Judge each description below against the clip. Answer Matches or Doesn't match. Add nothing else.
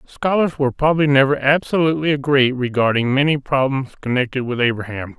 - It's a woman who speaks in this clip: Doesn't match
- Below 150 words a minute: Matches